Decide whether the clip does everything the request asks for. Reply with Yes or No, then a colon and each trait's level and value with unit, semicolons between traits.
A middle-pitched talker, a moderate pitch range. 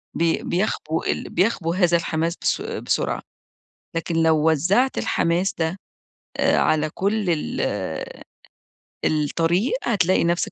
Yes: medium, 170 Hz; average, 3.0 semitones